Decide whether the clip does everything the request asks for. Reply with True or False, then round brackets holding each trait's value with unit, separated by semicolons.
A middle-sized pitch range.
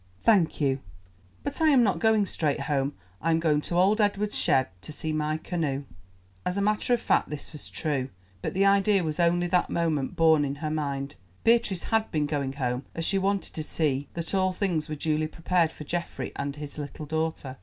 True (4.5 semitones)